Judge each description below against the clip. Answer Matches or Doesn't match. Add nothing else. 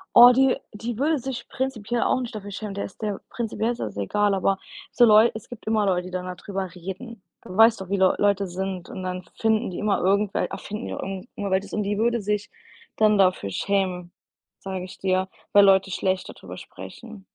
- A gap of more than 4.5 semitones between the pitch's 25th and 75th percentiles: Doesn't match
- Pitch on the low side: Doesn't match